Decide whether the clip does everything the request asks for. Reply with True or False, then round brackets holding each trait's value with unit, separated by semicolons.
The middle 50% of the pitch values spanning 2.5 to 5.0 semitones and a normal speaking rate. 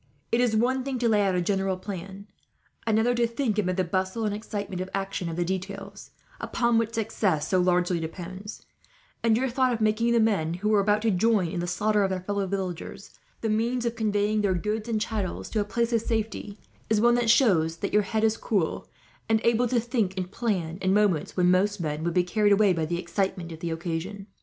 False (3.4 semitones; 225 wpm)